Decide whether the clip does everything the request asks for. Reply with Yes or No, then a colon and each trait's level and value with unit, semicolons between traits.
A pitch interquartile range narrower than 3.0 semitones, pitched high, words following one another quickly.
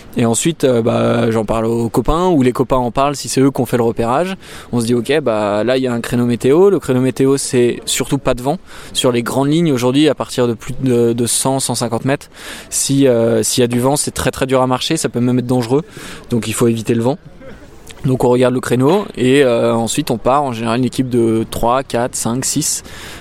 No: narrow, 2.6 semitones; low, 125 Hz; fast, 250 wpm